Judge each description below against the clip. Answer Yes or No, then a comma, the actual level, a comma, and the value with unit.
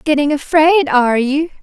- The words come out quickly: No, average, 150 wpm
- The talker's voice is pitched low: No, very high, 295 Hz